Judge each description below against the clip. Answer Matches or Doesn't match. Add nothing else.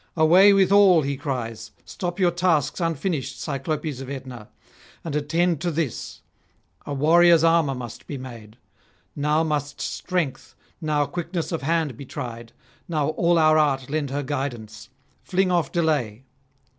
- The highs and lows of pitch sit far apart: Doesn't match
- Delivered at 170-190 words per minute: Doesn't match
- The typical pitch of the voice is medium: Matches